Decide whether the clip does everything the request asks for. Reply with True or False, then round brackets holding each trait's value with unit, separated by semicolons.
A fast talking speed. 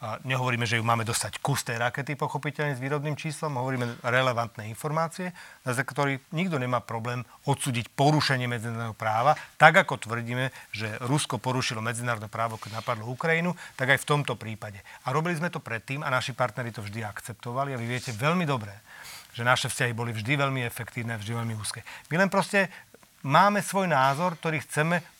True (180 wpm)